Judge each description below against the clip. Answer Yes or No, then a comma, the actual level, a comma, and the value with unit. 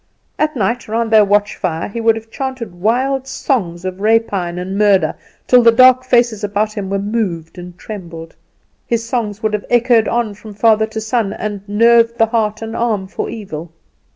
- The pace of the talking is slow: No, average, 185 wpm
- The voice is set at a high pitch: Yes, high, 220 Hz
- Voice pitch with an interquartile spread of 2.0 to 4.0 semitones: Yes, average, 2.9 semitones